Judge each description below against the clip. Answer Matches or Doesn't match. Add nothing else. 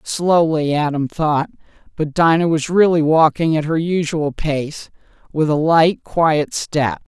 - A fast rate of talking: Doesn't match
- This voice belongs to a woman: Matches